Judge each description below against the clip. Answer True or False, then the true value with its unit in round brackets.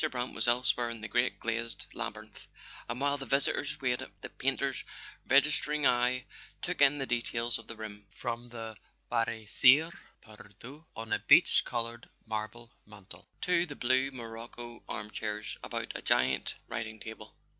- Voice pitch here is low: True (120 Hz)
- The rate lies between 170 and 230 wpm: False (155 wpm)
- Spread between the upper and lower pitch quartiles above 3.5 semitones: False (2.9 semitones)